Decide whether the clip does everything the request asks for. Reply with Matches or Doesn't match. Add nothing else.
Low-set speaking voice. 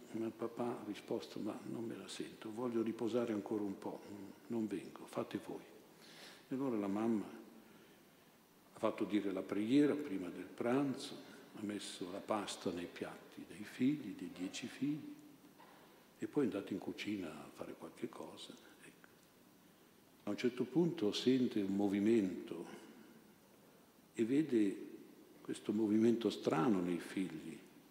Matches